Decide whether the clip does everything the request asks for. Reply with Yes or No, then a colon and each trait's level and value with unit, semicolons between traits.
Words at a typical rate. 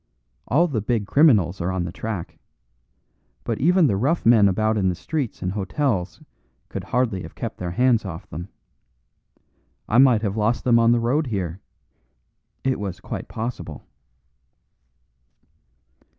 Yes: average, 150 wpm